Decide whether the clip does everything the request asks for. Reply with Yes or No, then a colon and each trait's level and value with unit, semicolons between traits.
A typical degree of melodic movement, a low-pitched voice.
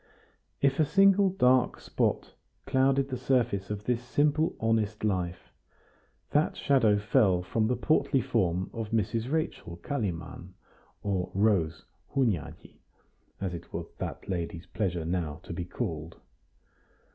No: wide, 6.5 semitones; low, 110 Hz